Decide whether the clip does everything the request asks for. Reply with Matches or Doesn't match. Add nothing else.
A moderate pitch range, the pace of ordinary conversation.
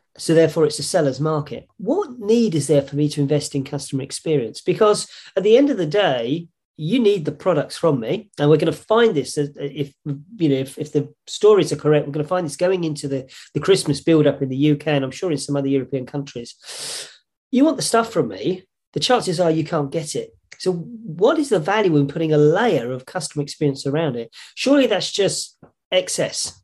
Doesn't match